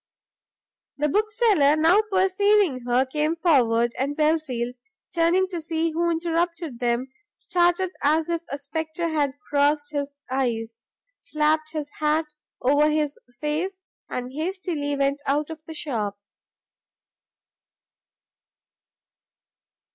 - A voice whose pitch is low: No, very high, 305 Hz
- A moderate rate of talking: No, slow, 110 wpm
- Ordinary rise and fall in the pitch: Yes, average, 3.2 semitones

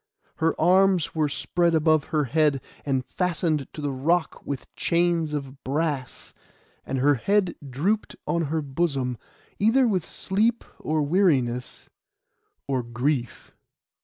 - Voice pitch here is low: No, medium, 155 Hz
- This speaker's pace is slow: Yes, slow, 130 wpm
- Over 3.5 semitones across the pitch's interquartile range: Yes, average, 4.2 semitones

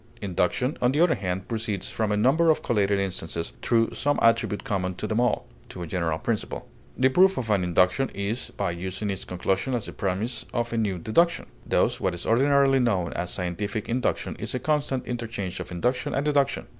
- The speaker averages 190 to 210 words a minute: Yes, average, 200 wpm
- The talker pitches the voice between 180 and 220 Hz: No, low, 110 Hz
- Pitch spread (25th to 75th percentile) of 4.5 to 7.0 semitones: Yes, wide, 5.5 semitones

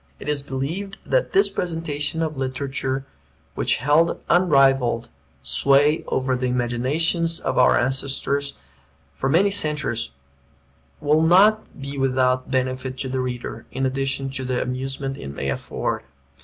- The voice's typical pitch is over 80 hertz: Yes, low, 135 Hz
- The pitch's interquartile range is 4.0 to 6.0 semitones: No, average, 3.0 semitones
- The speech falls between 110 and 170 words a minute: Yes, average, 140 wpm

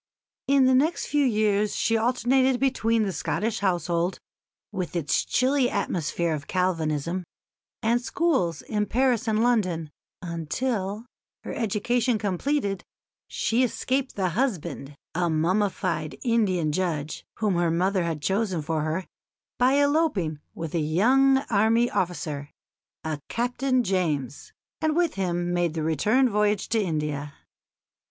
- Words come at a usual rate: No, slow, 130 wpm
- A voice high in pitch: Yes, high, 195 Hz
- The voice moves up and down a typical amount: No, wide, 6.3 semitones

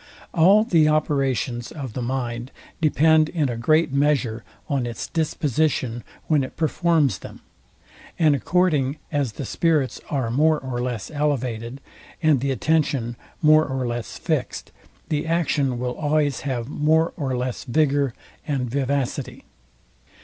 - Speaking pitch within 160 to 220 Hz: No, medium, 140 Hz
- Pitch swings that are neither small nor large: Yes, average, 3.7 semitones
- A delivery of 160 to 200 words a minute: No, slow, 135 wpm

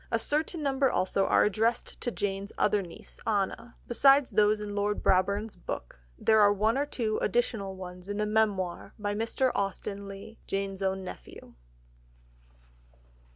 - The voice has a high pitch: Yes, high, 210 Hz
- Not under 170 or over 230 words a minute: No, average, 155 wpm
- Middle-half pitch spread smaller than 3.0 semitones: Yes, narrow, 2.5 semitones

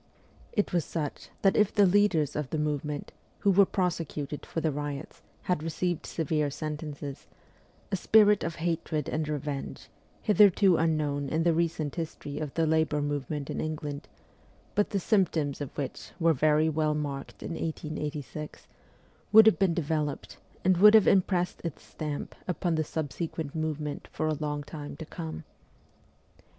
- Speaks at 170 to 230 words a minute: No, average, 155 wpm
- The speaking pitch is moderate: Yes, medium, 155 Hz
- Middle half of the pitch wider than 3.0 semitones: No, average, 2.7 semitones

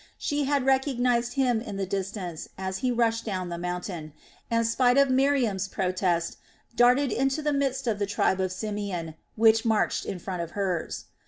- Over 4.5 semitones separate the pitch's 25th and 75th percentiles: Yes, average, 5.2 semitones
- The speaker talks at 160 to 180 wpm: Yes, average, 175 wpm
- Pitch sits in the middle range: No, high, 220 Hz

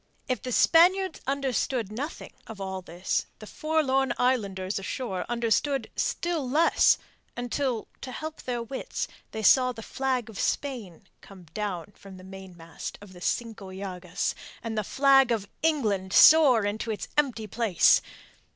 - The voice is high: Yes, high, 230 Hz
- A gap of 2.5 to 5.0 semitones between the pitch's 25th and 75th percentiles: No, wide, 5.5 semitones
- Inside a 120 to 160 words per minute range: Yes, average, 145 wpm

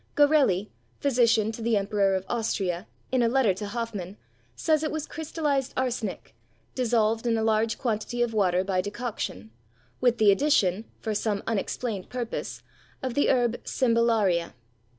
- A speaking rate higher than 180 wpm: No, average, 150 wpm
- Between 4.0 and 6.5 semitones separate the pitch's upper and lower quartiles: No, average, 3.6 semitones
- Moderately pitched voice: No, high, 225 Hz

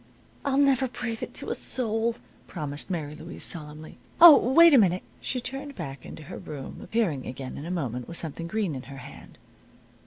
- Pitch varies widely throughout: Yes, wide, 9.0 semitones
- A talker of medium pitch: Yes, medium, 175 Hz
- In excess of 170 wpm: Yes, average, 190 wpm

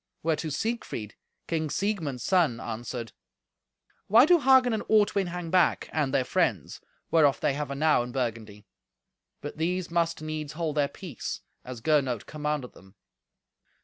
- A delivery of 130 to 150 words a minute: Yes, average, 145 wpm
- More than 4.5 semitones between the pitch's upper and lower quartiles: Yes, wide, 5.6 semitones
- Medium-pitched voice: Yes, medium, 155 Hz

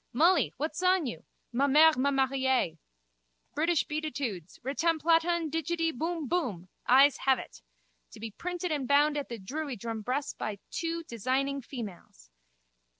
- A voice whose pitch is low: No, very high, 280 Hz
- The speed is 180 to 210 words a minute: No, slow, 135 wpm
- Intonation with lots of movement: No, average, 4.6 semitones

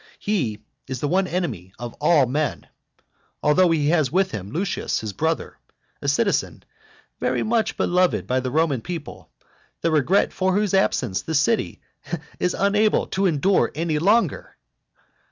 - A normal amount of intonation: No, wide, 6.1 semitones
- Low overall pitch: No, medium, 165 Hz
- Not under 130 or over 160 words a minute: Yes, average, 150 wpm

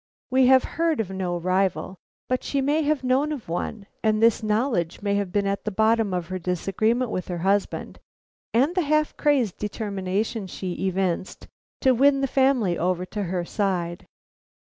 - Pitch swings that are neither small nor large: No, wide, 5.7 semitones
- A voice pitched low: No, high, 210 Hz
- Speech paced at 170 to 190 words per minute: Yes, average, 175 wpm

